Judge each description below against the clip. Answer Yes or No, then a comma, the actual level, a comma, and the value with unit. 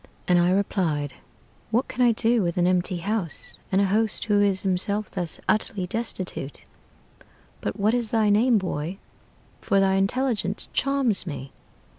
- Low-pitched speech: No, high, 195 Hz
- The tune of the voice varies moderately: Yes, average, 3.6 semitones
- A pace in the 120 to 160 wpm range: Yes, average, 155 wpm